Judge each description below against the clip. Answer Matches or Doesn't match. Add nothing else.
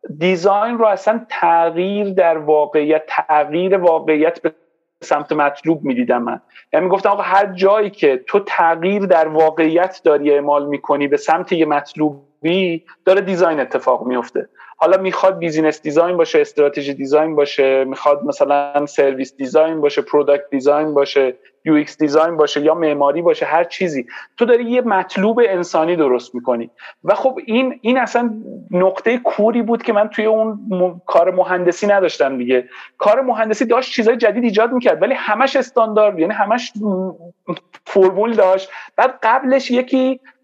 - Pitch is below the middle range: Doesn't match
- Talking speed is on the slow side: Doesn't match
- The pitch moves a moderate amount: Doesn't match